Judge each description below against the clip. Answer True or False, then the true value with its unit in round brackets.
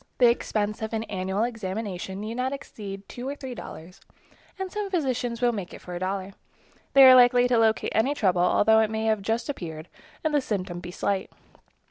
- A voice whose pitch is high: True (220 Hz)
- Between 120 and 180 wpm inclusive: False (200 wpm)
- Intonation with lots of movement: False (4.3 semitones)